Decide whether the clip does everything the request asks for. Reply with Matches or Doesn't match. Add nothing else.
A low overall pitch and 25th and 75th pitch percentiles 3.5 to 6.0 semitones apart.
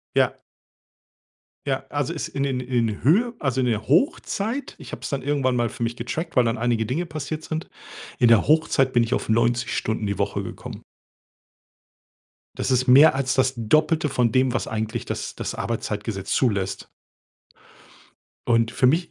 Matches